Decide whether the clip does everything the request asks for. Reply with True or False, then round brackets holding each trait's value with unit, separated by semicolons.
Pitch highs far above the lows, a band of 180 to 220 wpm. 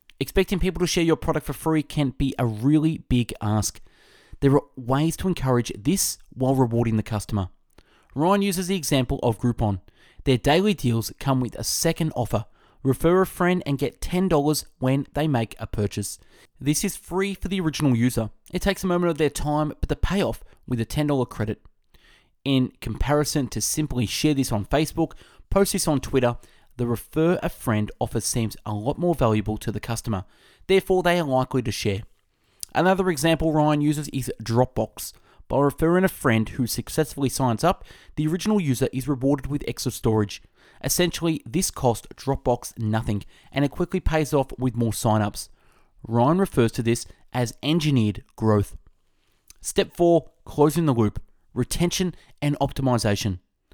False (5.8 semitones; 170 wpm)